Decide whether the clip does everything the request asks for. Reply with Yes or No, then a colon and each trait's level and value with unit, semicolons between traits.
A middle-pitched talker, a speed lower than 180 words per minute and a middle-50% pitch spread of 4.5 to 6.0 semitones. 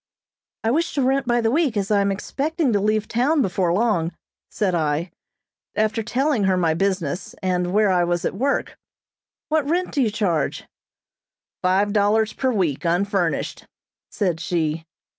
No: high, 205 Hz; average, 160 wpm; average, 5.2 semitones